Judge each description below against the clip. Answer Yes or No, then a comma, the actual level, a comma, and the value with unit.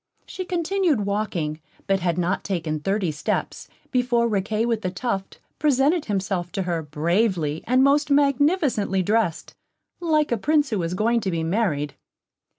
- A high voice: Yes, high, 210 Hz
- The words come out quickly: No, average, 155 wpm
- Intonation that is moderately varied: No, wide, 7.3 semitones